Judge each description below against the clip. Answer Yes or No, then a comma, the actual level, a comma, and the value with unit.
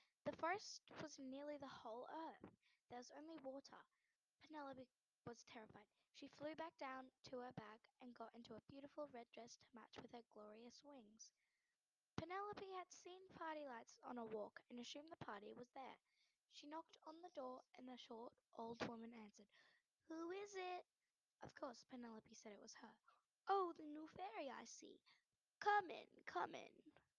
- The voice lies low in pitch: No, very high, 270 Hz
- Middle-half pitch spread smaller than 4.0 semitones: No, wide, 5.6 semitones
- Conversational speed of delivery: Yes, average, 175 wpm